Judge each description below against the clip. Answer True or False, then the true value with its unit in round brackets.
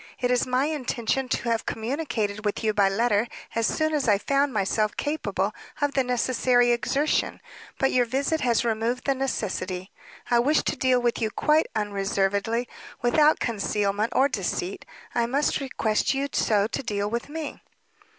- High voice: True (240 Hz)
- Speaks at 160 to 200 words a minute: True (165 wpm)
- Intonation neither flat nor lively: True (4.1 semitones)